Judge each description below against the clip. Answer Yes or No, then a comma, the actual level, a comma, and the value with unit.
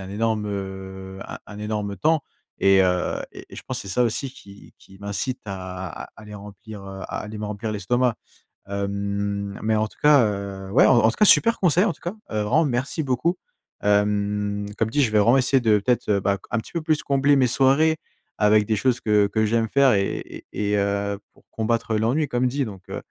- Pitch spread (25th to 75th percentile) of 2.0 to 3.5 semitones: No, average, 3.9 semitones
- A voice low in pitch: Yes, low, 105 Hz